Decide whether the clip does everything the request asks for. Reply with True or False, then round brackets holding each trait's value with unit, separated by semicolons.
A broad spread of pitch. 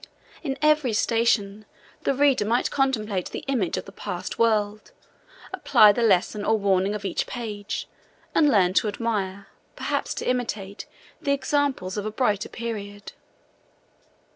False (3.5 semitones)